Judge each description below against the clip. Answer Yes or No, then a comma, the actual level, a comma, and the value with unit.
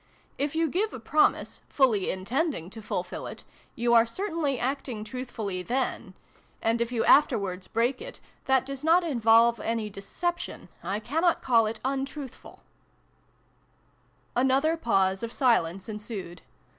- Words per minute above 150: No, slow, 135 wpm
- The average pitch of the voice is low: No, high, 240 Hz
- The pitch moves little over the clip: No, average, 4.5 semitones